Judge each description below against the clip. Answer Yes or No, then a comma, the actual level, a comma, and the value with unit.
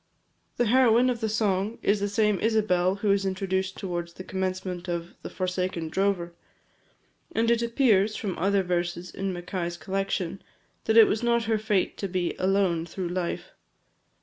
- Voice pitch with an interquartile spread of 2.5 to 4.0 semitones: Yes, average, 2.9 semitones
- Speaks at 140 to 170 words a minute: Yes, average, 165 wpm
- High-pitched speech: Yes, high, 195 Hz